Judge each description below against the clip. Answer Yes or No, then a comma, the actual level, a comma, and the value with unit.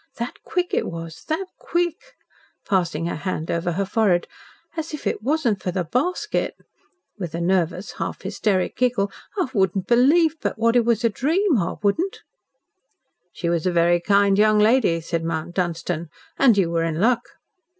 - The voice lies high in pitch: Yes, high, 200 Hz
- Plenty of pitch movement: Yes, wide, 6.4 semitones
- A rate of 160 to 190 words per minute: Yes, average, 170 wpm